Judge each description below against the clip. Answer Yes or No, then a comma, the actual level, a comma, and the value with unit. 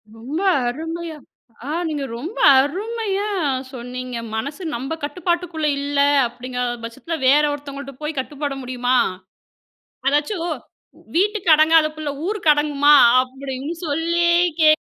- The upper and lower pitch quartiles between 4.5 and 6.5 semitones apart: No, average, 3.8 semitones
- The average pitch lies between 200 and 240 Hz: No, very high, 295 Hz